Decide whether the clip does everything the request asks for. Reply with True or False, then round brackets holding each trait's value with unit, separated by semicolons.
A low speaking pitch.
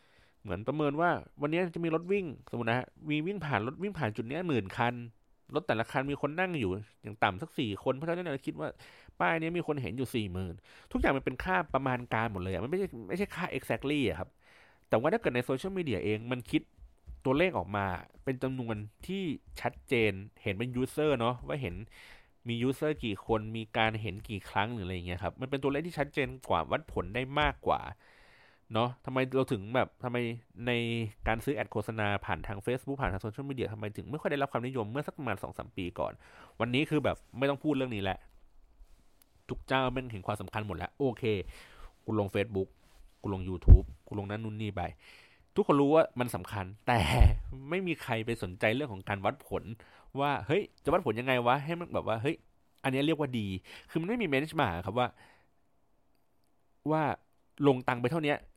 True (120 Hz)